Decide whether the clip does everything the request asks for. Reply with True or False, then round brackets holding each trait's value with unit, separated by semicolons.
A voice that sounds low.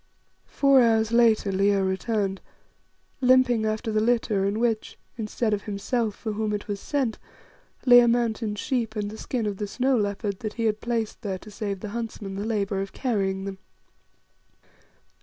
False (215 Hz)